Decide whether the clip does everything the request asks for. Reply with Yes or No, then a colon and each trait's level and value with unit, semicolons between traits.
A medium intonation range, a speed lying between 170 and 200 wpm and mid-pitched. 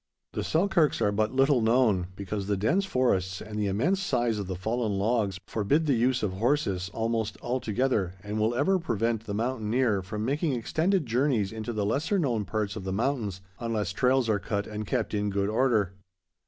No: average, 4.1 semitones; average, 190 wpm; low, 110 Hz